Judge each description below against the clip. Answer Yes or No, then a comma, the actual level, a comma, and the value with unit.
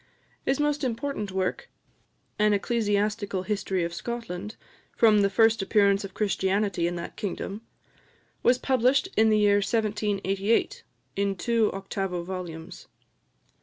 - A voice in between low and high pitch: No, high, 205 Hz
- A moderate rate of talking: No, slow, 125 wpm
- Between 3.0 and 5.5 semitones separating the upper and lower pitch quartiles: No, narrow, 2.6 semitones